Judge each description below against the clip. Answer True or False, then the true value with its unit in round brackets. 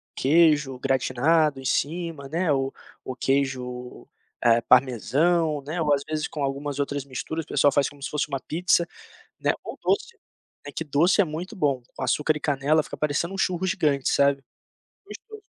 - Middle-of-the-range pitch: True (145 Hz)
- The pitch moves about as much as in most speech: True (3.2 semitones)